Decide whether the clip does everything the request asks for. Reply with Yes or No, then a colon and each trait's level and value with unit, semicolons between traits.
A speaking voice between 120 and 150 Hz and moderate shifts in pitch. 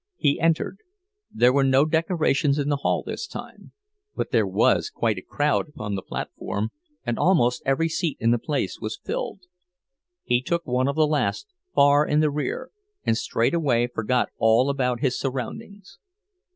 Yes: medium, 140 Hz; average, 4.4 semitones